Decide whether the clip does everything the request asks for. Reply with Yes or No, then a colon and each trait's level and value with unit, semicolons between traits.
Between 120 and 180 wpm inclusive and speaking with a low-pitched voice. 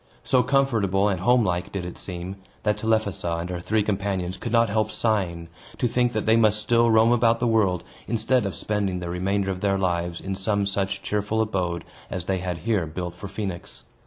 No: fast, 205 wpm; low, 100 Hz